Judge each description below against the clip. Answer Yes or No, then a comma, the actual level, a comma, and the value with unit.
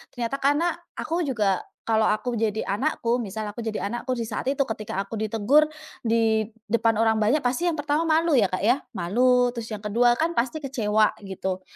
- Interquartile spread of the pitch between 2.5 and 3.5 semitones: No, average, 4.1 semitones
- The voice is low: No, high, 230 Hz